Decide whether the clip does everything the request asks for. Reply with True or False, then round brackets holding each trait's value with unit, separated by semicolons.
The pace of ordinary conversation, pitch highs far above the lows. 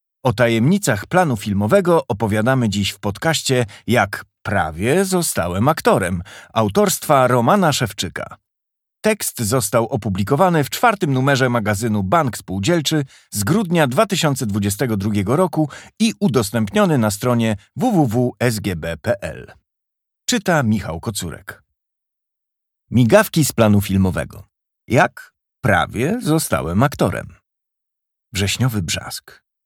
False (95 wpm; 7.3 semitones)